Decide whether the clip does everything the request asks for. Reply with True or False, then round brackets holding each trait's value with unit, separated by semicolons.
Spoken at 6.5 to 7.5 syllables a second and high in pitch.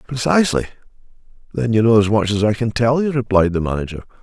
False (6.7 syllables/s; 110 Hz)